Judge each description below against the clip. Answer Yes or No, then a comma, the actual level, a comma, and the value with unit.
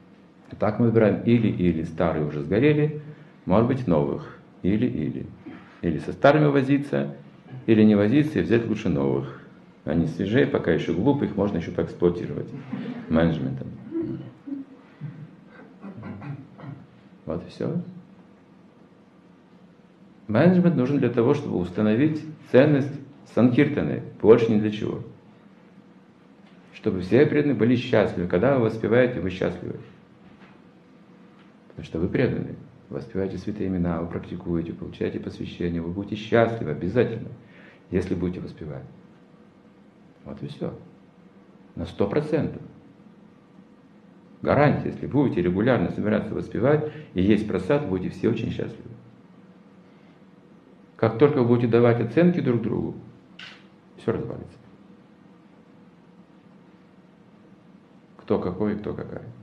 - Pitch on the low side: Yes, low, 115 Hz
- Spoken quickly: No, average, 115 wpm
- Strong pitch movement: Yes, wide, 8.0 semitones